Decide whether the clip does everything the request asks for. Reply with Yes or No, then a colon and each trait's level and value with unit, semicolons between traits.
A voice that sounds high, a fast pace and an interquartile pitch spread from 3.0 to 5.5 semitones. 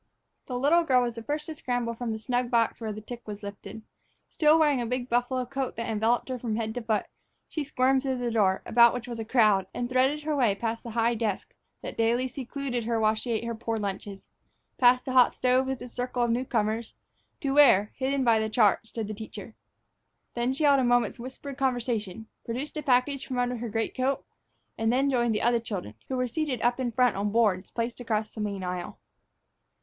No: high, 240 Hz; fast, 220 wpm; narrow, 2.6 semitones